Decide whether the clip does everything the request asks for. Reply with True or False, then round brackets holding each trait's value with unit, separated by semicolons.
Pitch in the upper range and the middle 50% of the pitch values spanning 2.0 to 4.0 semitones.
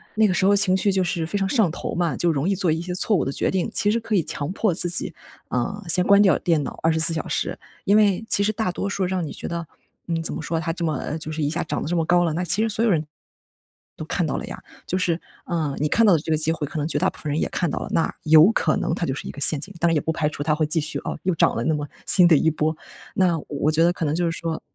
False (170 Hz; 3.1 semitones)